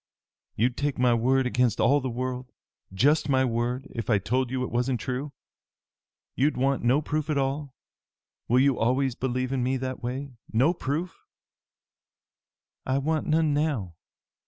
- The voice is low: Yes, low, 130 Hz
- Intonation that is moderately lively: No, narrow, 2.3 semitones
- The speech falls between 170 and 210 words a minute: No, average, 160 wpm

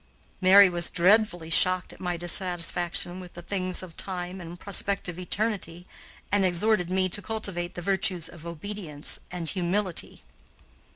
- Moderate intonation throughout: No, narrow, 2.0 semitones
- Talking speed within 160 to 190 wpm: No, average, 140 wpm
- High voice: No, medium, 180 Hz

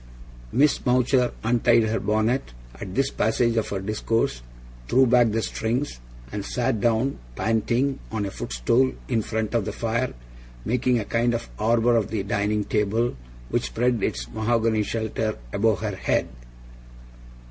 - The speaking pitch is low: Yes, low, 115 Hz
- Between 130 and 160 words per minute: Yes, average, 150 wpm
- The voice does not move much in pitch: Yes, narrow, 2.3 semitones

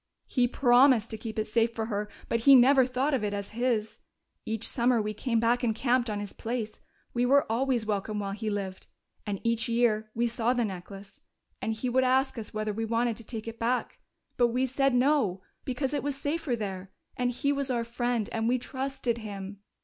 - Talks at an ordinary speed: No, fast, 210 wpm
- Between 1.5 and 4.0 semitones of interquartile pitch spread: Yes, average, 2.9 semitones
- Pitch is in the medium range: No, high, 235 Hz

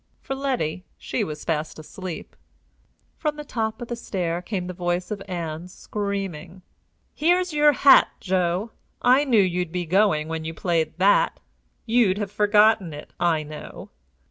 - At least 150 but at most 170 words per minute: Yes, average, 155 wpm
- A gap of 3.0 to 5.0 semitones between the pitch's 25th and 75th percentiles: Yes, average, 4.7 semitones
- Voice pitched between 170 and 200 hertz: Yes, medium, 185 Hz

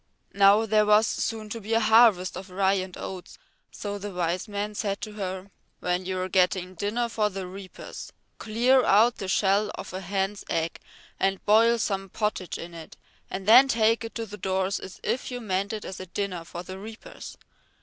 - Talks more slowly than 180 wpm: No, average, 200 wpm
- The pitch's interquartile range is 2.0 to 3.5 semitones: Yes, narrow, 2.6 semitones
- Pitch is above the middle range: Yes, high, 200 Hz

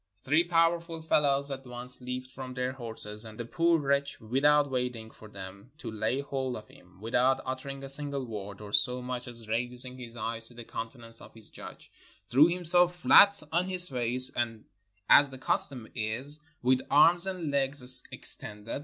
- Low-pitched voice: Yes, low, 130 Hz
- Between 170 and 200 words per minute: Yes, average, 175 wpm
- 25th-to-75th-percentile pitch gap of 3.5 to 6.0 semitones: Yes, average, 3.8 semitones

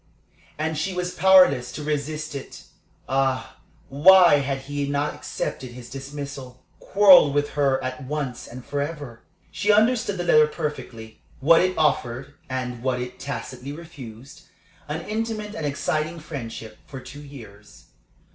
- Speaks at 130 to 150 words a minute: Yes, average, 140 wpm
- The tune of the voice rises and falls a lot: No, average, 3.8 semitones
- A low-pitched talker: No, medium, 145 Hz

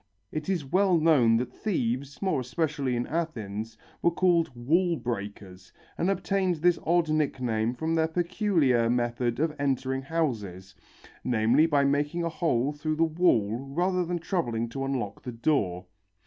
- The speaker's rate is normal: Yes, average, 150 wpm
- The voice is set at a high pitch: No, medium, 140 Hz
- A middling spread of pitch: No, wide, 5.8 semitones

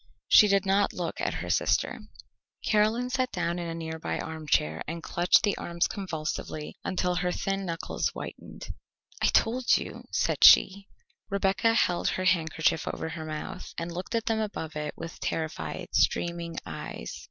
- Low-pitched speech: No, medium, 175 Hz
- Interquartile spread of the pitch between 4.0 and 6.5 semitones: No, average, 3.6 semitones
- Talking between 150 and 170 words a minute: Yes, average, 160 wpm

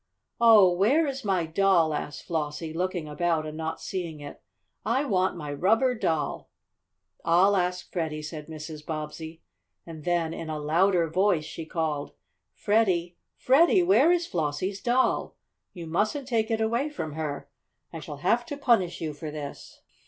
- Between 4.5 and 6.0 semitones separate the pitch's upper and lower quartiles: Yes, average, 5.3 semitones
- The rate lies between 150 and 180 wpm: Yes, average, 160 wpm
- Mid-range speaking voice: Yes, medium, 170 Hz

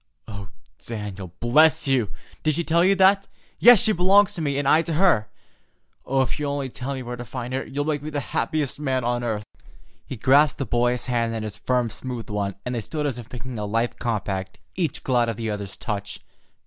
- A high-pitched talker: No, low, 125 Hz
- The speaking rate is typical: No, fast, 220 wpm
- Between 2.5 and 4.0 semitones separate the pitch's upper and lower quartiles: No, average, 4.7 semitones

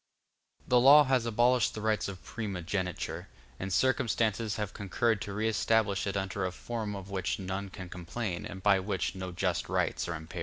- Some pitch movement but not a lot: Yes, average, 3.1 semitones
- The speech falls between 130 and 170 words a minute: No, average, 185 wpm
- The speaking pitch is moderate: No, low, 100 Hz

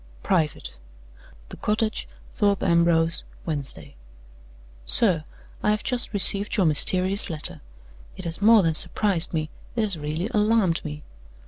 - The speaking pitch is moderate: Yes, medium, 180 Hz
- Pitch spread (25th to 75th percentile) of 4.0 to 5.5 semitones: Yes, average, 4.7 semitones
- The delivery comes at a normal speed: No, slow, 125 wpm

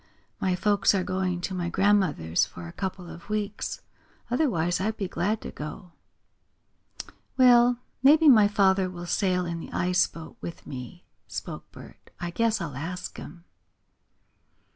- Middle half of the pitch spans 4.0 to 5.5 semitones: No, average, 3.3 semitones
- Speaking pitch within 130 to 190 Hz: Yes, medium, 185 Hz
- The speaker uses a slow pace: No, average, 150 wpm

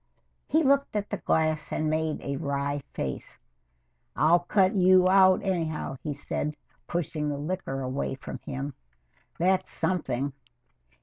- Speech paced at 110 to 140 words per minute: Yes, slow, 135 wpm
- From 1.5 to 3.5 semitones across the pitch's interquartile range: No, average, 4.7 semitones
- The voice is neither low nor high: Yes, medium, 155 Hz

